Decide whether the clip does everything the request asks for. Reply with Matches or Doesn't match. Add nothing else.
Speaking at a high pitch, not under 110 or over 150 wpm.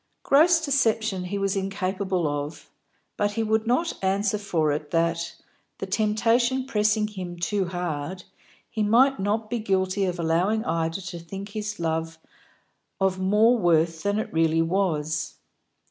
Matches